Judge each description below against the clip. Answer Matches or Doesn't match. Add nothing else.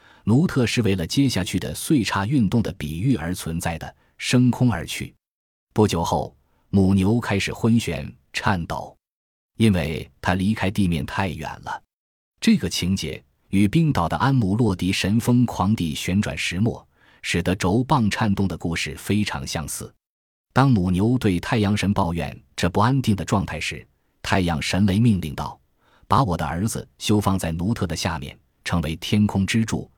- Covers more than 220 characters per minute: Matches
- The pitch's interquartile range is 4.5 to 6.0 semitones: Matches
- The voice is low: Matches